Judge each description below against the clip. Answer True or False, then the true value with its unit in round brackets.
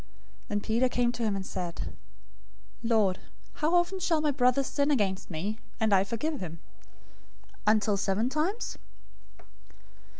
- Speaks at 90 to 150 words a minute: True (140 wpm)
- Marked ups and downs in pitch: True (6.3 semitones)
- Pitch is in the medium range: False (230 Hz)